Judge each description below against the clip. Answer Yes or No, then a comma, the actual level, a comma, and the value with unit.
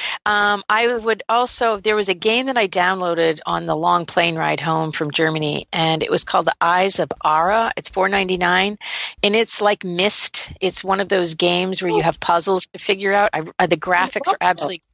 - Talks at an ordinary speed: No, fast, 220 wpm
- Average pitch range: Yes, average, 3.2 semitones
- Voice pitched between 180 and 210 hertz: Yes, medium, 185 Hz